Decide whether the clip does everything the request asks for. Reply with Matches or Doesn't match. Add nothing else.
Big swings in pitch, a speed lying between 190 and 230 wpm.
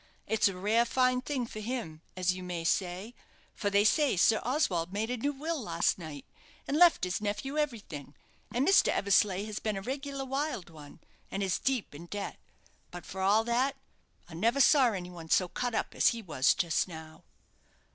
Matches